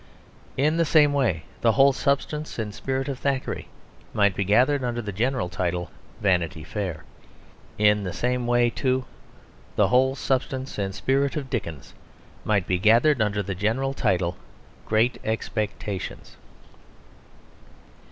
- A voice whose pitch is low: Yes, low, 115 Hz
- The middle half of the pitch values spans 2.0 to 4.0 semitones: No, average, 5.0 semitones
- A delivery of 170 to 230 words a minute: No, slow, 135 wpm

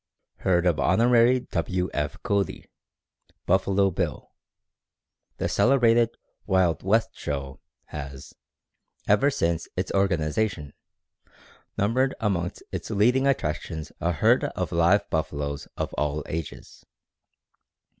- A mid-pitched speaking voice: No, very low, 90 Hz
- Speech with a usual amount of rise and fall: No, wide, 6.0 semitones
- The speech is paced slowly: Yes, slow, 105 wpm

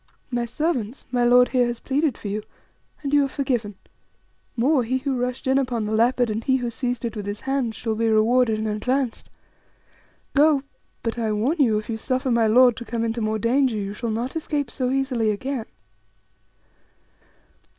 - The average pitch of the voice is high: Yes, high, 245 Hz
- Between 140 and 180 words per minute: No, average, 190 wpm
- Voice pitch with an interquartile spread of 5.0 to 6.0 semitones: No, average, 3.0 semitones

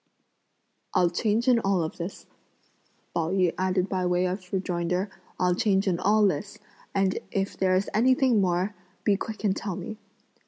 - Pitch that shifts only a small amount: Yes, narrow, 2.3 semitones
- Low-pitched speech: No, high, 190 Hz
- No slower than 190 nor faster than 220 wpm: No, average, 155 wpm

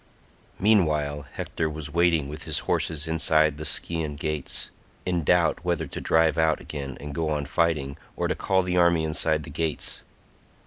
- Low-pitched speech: Yes, very low, 80 Hz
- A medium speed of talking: Yes, average, 170 wpm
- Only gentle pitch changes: Yes, narrow, 2.1 semitones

